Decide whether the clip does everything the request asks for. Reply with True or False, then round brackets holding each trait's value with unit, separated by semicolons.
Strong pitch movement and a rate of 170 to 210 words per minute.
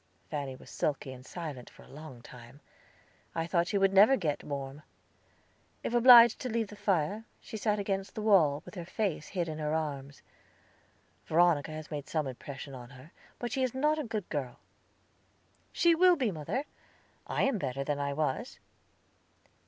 True (7.0 semitones; 175 wpm)